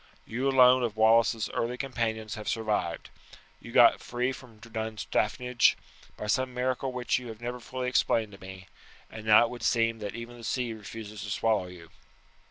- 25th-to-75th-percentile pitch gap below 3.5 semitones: Yes, narrow, 2.5 semitones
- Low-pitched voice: Yes, low, 115 Hz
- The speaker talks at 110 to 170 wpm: No, average, 180 wpm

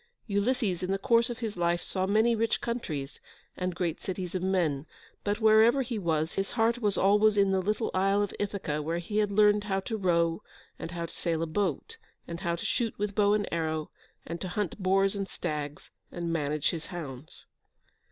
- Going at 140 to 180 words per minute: No, average, 200 wpm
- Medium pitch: No, high, 195 Hz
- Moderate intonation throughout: Yes, average, 3.8 semitones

